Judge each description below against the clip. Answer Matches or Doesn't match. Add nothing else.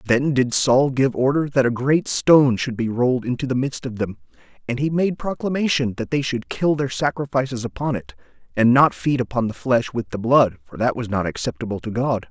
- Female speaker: Doesn't match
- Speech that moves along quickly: Matches